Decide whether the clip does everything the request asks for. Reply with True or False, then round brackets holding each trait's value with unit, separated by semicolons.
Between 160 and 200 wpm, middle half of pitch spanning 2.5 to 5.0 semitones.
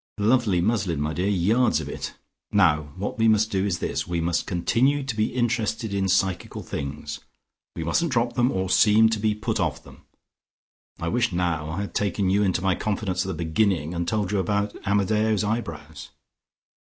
True (190 wpm; 4.1 semitones)